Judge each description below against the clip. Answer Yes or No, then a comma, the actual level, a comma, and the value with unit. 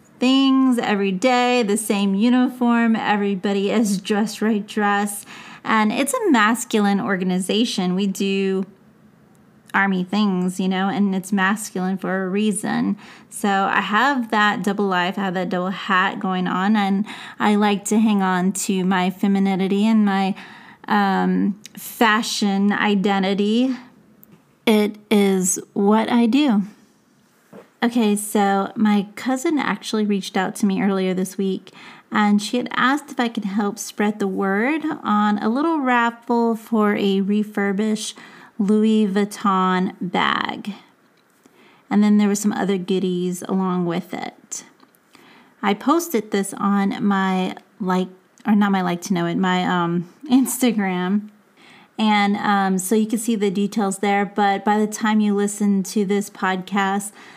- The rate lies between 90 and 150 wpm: Yes, average, 145 wpm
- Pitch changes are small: Yes, narrow, 2.2 semitones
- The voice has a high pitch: Yes, high, 205 Hz